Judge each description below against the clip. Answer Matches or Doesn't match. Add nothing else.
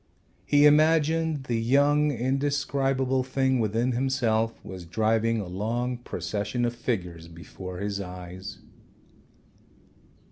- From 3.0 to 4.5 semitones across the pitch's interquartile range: Doesn't match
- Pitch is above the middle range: Doesn't match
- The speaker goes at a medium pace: Doesn't match